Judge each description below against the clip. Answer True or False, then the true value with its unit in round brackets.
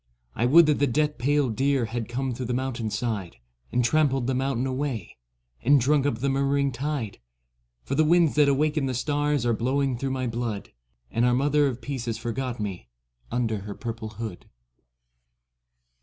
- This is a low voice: True (130 Hz)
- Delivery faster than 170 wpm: True (180 wpm)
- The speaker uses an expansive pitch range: False (3.4 semitones)